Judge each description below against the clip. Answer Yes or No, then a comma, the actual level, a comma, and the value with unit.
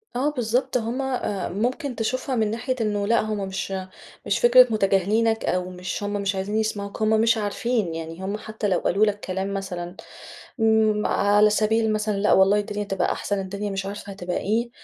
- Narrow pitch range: Yes, narrow, 2.3 semitones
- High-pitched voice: Yes, high, 210 Hz